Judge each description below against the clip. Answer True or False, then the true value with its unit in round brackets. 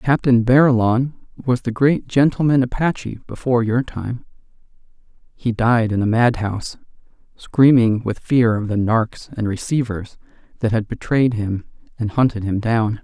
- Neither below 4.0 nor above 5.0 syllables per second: True (4.6 syllables/s)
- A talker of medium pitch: False (120 Hz)